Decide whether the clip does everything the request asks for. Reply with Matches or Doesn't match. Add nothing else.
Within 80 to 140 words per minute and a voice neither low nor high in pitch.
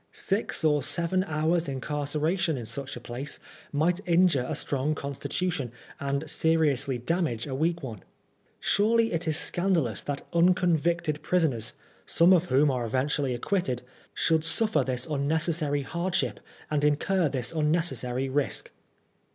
Matches